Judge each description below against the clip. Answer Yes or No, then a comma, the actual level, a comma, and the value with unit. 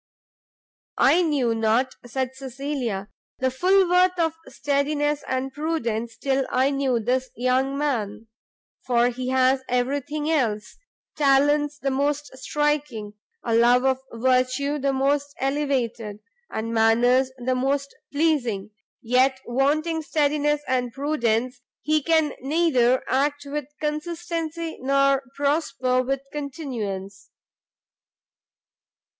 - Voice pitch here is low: No, very high, 270 Hz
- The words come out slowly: Yes, slow, 115 wpm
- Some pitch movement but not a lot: Yes, average, 3.1 semitones